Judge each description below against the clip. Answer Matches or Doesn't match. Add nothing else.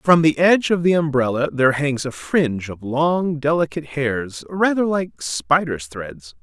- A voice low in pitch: Doesn't match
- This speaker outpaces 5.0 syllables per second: Doesn't match